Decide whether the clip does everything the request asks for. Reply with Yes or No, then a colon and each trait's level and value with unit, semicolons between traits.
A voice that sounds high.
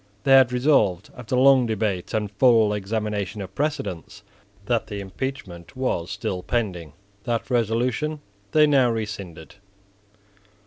No: low, 110 Hz